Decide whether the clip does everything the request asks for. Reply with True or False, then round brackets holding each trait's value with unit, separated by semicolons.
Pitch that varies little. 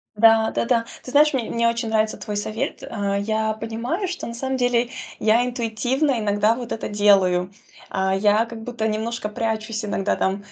True (2.2 semitones)